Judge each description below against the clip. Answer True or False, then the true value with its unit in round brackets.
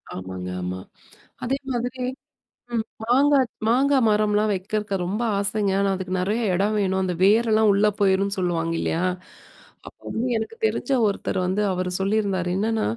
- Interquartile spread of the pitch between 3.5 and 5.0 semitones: False (3.0 semitones)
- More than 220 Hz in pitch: False (205 Hz)